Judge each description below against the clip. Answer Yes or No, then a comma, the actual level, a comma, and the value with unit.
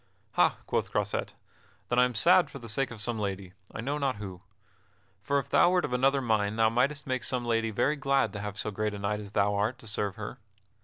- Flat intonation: No, average, 4.6 semitones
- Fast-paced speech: Yes, fast, 240 wpm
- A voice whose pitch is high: No, low, 115 Hz